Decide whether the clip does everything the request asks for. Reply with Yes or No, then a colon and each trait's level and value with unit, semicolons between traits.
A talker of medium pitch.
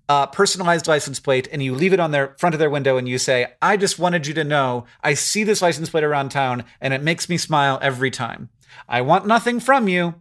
Yes: medium, 155 Hz